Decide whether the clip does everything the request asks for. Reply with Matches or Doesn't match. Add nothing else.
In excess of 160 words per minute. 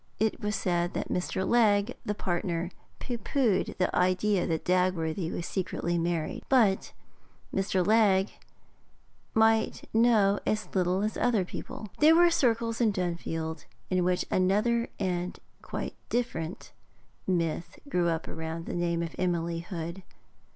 Doesn't match